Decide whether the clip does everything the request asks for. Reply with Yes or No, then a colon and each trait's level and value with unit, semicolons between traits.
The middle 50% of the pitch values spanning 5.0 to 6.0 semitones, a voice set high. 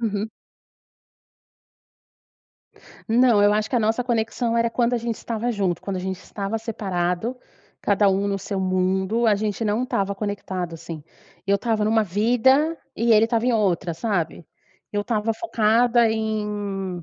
No: average, 2.9 semitones; high, 210 Hz